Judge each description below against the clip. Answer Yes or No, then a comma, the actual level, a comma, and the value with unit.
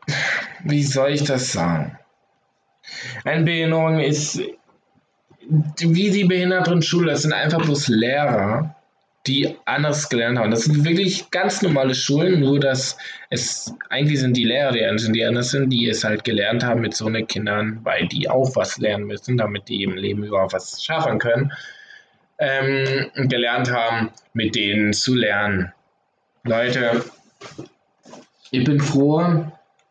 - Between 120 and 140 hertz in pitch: Yes, low, 135 Hz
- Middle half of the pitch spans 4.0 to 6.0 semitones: Yes, average, 5.1 semitones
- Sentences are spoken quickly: No, average, 140 wpm